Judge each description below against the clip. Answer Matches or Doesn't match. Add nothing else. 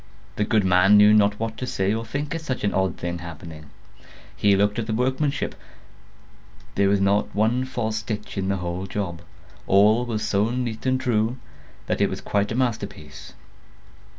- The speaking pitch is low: Matches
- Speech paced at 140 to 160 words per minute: Doesn't match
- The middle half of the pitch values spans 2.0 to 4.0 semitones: Matches